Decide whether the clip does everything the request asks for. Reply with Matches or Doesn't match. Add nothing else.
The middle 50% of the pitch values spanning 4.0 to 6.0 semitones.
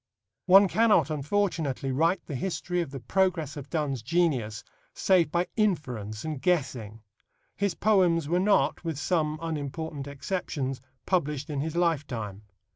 Matches